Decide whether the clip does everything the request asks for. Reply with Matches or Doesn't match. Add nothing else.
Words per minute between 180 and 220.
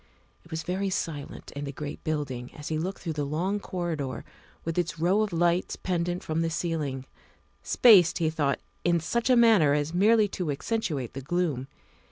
Matches